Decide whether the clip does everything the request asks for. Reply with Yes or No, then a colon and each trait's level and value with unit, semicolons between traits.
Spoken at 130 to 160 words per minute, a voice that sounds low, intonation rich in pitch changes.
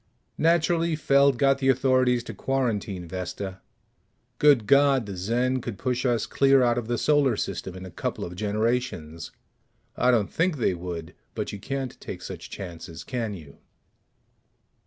Yes: average, 155 wpm; low, 120 Hz; wide, 6.1 semitones